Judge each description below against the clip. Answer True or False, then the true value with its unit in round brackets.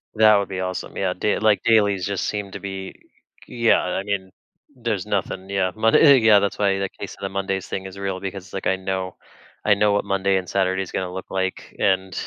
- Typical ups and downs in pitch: False (1.4 semitones)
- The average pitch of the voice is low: True (95 Hz)